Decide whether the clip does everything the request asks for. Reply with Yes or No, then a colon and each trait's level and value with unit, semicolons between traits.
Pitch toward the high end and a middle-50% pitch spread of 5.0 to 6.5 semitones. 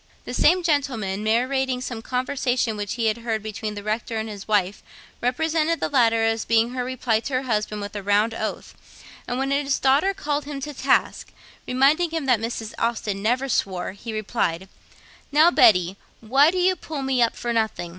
No: high, 235 Hz; average, 4.2 semitones